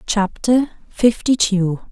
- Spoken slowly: Yes, slow, 95 wpm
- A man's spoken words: No, female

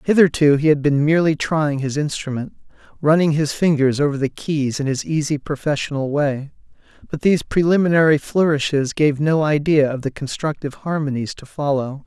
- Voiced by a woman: No, male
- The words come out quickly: No, average, 160 wpm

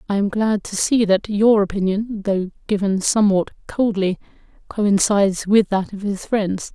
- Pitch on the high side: Yes, high, 200 Hz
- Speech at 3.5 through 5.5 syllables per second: Yes, 4.5 syllables/s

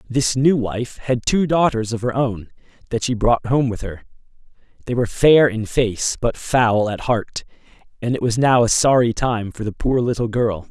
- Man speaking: Yes, male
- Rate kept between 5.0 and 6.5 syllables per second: No, 4.6 syllables/s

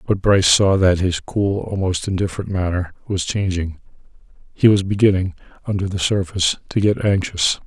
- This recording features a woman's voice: No, male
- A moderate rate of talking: Yes, average, 150 wpm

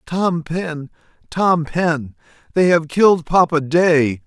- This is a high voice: No, medium, 160 Hz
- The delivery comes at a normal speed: No, slow, 125 wpm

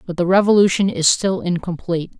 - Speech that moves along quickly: No, average, 165 wpm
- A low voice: No, medium, 180 Hz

